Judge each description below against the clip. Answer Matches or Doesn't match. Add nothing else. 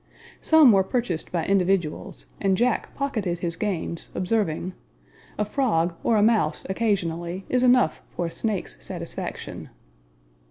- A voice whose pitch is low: Doesn't match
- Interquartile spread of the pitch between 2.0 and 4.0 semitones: Doesn't match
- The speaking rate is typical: Doesn't match